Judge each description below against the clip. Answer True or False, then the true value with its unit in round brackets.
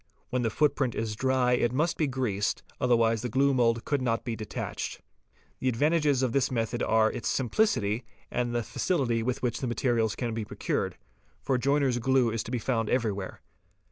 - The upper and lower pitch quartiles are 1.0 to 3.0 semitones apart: True (2.5 semitones)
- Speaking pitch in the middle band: False (120 Hz)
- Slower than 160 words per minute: False (185 wpm)